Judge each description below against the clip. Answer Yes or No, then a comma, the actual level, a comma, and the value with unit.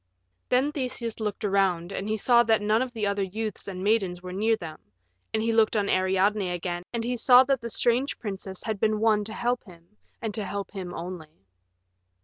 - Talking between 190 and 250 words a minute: Yes, fast, 205 wpm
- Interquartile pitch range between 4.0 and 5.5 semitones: No, average, 3.3 semitones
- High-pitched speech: Yes, high, 210 Hz